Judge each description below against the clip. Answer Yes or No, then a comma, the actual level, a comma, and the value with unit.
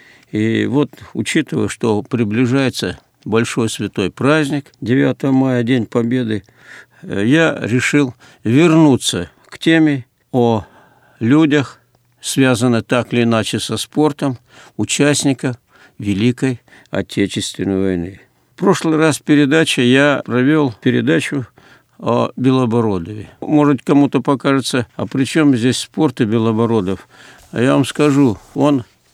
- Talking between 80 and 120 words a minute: Yes, slow, 110 wpm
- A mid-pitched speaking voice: No, low, 130 Hz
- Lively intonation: No, average, 4.0 semitones